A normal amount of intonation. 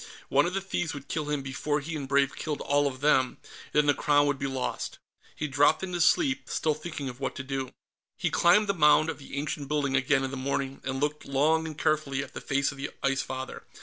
No: narrow, 2.2 semitones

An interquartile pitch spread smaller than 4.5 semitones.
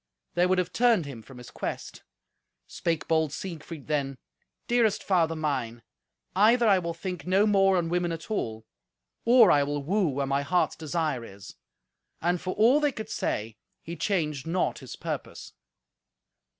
No: average, 5.3 semitones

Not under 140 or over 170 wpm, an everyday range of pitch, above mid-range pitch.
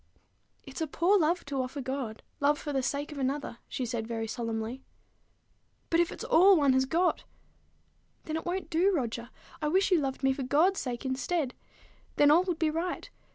No: average, 195 wpm; average, 4.3 semitones; very high, 285 Hz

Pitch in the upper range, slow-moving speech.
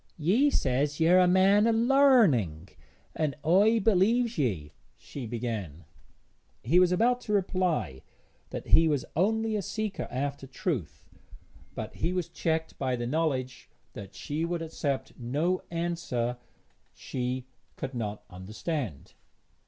No: medium, 160 Hz; slow, 130 wpm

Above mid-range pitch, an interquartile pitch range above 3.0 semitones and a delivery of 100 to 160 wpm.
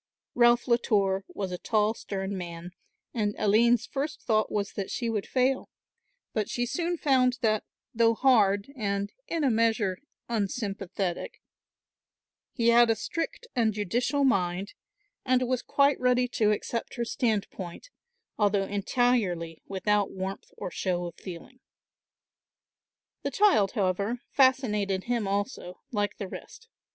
Yes: high, 215 Hz; average, 4.0 semitones; slow, 135 wpm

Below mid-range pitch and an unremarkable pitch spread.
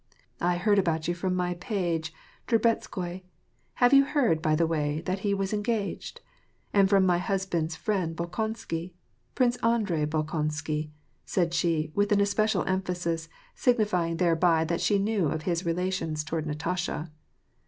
No: medium, 180 Hz; average, 3.7 semitones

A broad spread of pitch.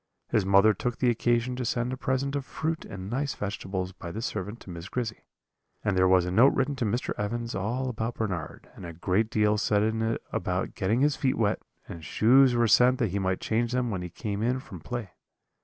No: average, 4.3 semitones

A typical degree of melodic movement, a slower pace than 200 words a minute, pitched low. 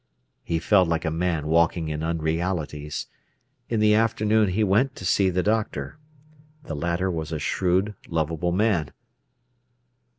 Yes: average, 4.3 semitones; average, 140 wpm; very low, 85 Hz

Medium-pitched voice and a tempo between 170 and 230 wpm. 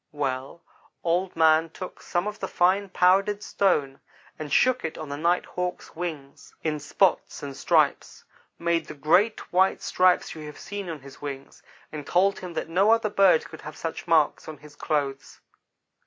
Yes: medium, 165 Hz; average, 175 wpm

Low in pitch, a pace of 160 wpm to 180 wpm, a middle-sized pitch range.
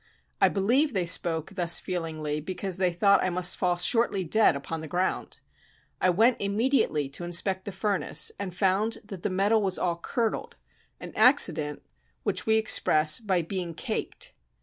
No: medium, 185 Hz; average, 165 wpm; average, 3.3 semitones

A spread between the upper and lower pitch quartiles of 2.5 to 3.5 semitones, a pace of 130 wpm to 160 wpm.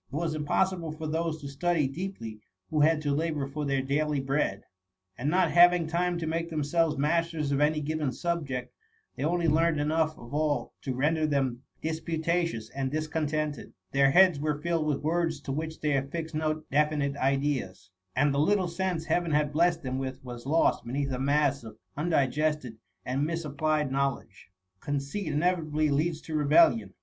No: average, 2.8 semitones; average, 170 wpm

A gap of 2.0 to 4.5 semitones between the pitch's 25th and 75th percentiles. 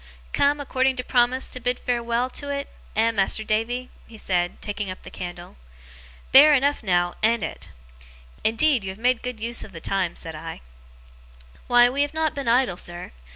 No: average, 5.0 semitones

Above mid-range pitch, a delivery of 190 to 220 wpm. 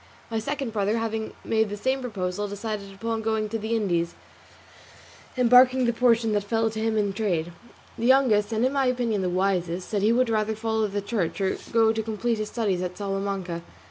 Yes: high, 220 Hz; average, 200 wpm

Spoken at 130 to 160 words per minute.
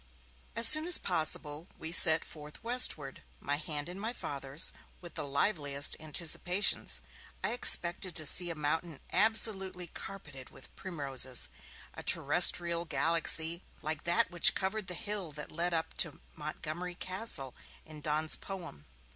Yes: average, 140 wpm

